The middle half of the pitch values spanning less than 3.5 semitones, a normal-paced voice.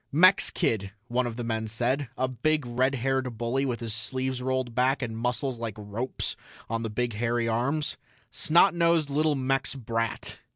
Yes: average, 2.7 semitones; average, 175 wpm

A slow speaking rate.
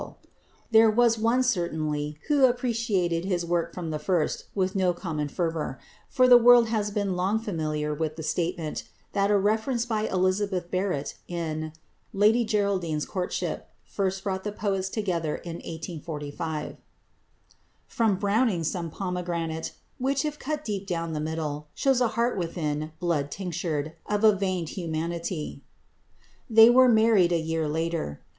No: average, 150 wpm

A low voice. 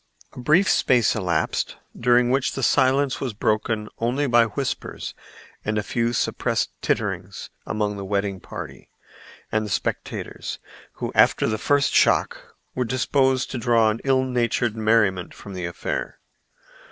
Yes: low, 115 Hz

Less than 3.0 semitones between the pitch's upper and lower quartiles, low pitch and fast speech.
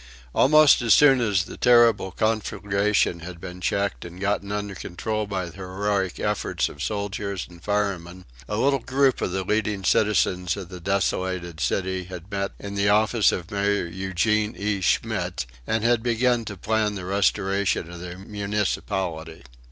No: narrow, 2.6 semitones; low, 100 Hz; average, 165 wpm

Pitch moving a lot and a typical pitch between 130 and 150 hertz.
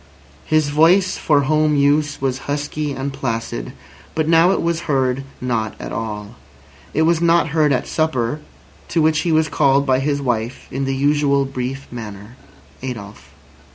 No: average, 3.6 semitones; medium, 140 Hz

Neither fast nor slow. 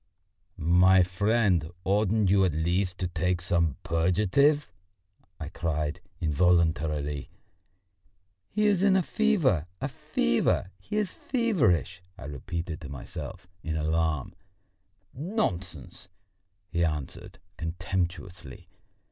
No: slow, 105 wpm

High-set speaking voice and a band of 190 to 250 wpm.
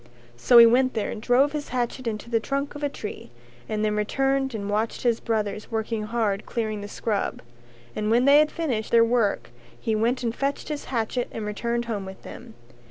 Yes: high, 230 Hz; fast, 205 wpm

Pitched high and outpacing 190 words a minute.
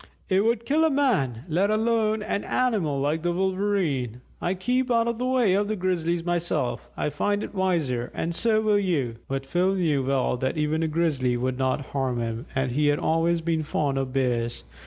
No: medium, 165 Hz; average, 200 wpm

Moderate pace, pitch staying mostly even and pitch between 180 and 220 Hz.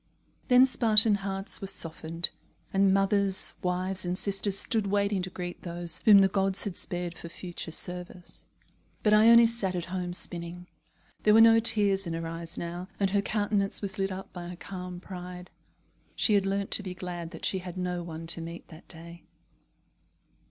Yes: average, 180 wpm; narrow, 2.3 semitones; medium, 185 Hz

